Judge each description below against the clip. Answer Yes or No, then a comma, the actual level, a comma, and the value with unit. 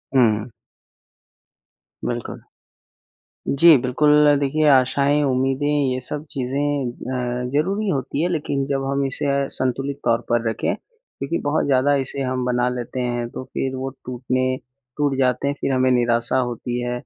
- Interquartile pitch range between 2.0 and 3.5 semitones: Yes, narrow, 2.4 semitones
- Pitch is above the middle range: No, low, 135 Hz